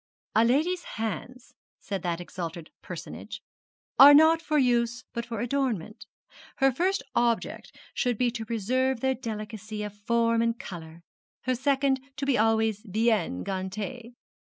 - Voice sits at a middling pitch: No, high, 230 Hz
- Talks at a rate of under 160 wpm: Yes, average, 140 wpm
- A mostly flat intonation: No, average, 3.6 semitones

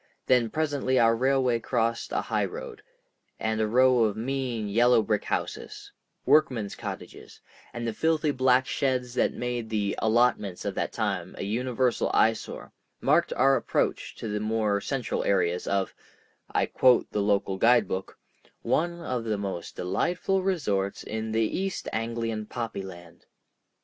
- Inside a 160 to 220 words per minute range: No, average, 140 wpm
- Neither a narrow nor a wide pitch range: Yes, average, 3.6 semitones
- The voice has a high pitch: No, low, 115 Hz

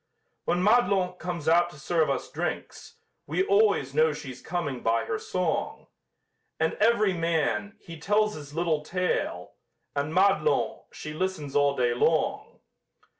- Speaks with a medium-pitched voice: Yes, medium, 165 Hz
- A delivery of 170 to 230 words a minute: No, average, 140 wpm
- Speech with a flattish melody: No, average, 4.2 semitones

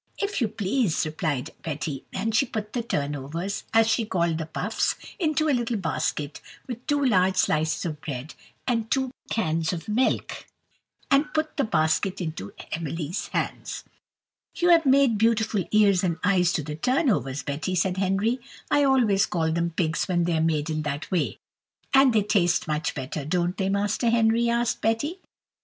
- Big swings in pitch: Yes, wide, 6.6 semitones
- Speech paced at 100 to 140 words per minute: No, average, 170 wpm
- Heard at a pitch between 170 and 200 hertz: Yes, high, 190 Hz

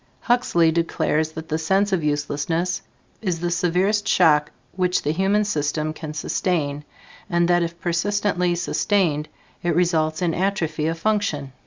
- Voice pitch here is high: No, medium, 170 Hz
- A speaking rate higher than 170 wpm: No, average, 145 wpm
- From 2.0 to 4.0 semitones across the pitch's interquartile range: Yes, average, 2.9 semitones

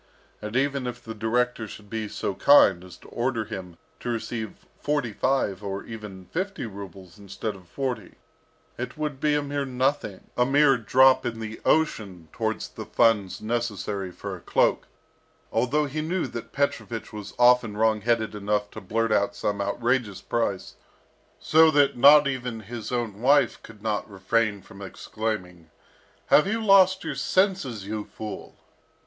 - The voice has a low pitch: Yes, low, 115 Hz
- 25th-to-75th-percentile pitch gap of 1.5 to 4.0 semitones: No, average, 4.5 semitones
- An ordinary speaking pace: Yes, average, 160 wpm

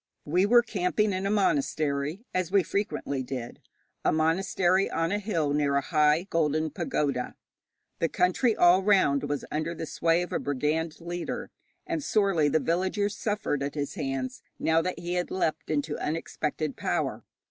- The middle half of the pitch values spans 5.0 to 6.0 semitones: No, average, 4.2 semitones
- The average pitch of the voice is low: No, medium, 165 Hz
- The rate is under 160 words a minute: No, average, 165 wpm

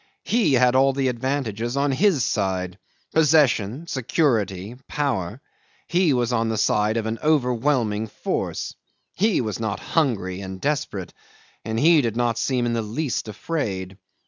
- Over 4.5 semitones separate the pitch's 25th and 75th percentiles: Yes, average, 5.1 semitones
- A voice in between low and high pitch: No, low, 120 Hz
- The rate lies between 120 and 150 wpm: Yes, average, 145 wpm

